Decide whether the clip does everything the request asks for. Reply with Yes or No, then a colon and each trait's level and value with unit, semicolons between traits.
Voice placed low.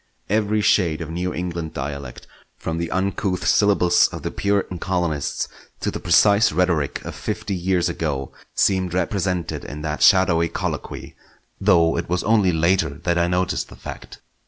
Yes: very low, 90 Hz